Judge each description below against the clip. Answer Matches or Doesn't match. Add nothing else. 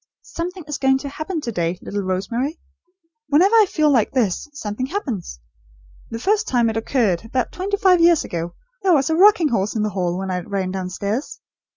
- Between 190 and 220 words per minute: Matches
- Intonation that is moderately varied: Doesn't match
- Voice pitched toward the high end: Matches